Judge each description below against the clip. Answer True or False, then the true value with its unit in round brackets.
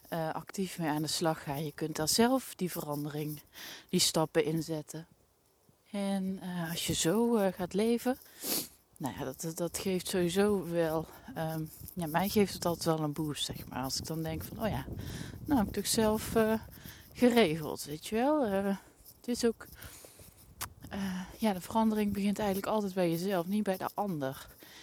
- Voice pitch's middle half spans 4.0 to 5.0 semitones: True (4.4 semitones)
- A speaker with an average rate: True (185 wpm)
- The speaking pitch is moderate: True (175 Hz)